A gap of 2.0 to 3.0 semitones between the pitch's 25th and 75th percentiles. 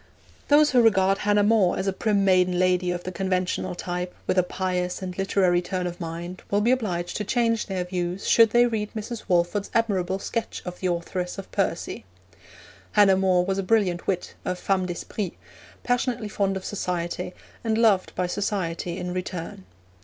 Yes: narrow, 2.6 semitones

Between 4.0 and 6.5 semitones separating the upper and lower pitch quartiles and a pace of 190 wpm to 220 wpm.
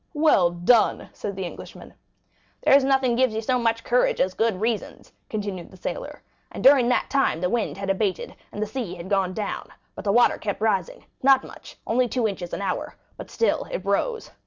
Yes: average, 4.6 semitones; average, 200 wpm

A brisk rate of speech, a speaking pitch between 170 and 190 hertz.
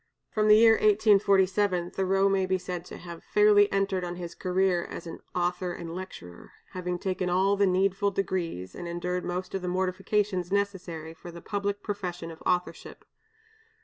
No: average, 165 wpm; medium, 185 Hz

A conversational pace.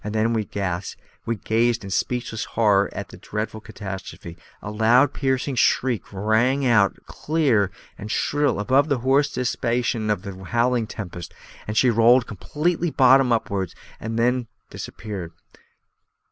No: slow, 130 wpm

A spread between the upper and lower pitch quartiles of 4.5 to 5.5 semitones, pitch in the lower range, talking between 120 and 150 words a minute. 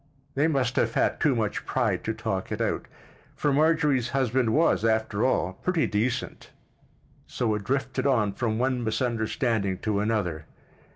No: average, 3.9 semitones; low, 120 Hz; average, 140 wpm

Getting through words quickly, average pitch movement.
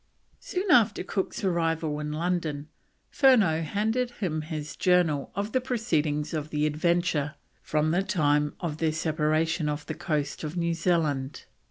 No: average, 150 wpm; average, 3.4 semitones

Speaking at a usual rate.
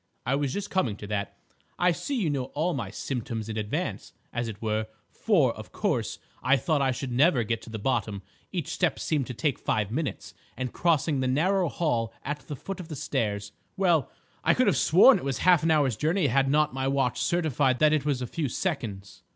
No: fast, 215 wpm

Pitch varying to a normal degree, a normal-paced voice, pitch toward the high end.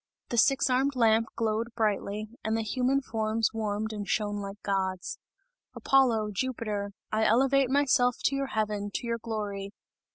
Yes: average, 3.2 semitones; average, 155 wpm; high, 220 Hz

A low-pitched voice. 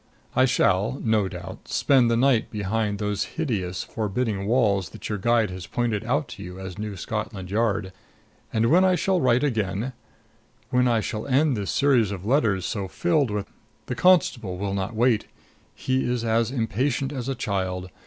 Yes: low, 110 Hz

